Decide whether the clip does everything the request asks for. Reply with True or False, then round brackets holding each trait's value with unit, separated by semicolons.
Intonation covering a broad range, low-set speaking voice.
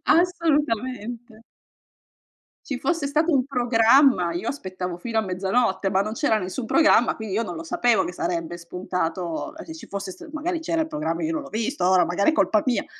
False (7.8 semitones; 230 Hz)